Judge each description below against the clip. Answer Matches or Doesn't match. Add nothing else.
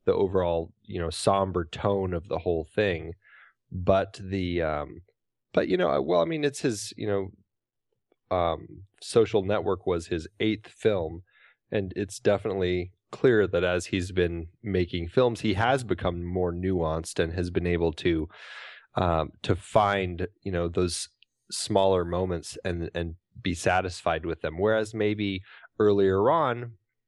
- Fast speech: Doesn't match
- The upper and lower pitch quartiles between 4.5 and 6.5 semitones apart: Doesn't match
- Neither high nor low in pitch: Doesn't match